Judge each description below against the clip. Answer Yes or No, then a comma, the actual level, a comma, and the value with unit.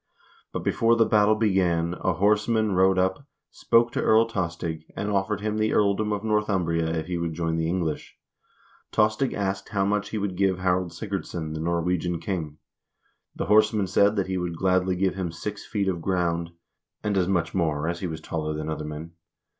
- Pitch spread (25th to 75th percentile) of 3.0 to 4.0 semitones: Yes, average, 3.7 semitones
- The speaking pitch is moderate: No, very low, 95 Hz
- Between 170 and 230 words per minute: Yes, average, 190 wpm